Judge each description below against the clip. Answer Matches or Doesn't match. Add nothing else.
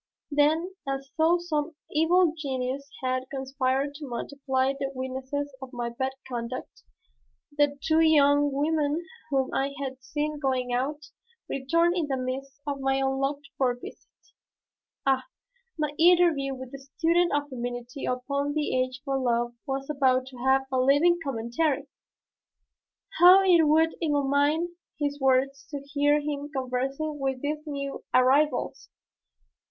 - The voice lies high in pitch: Matches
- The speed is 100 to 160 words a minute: Matches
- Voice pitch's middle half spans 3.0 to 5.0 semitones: Doesn't match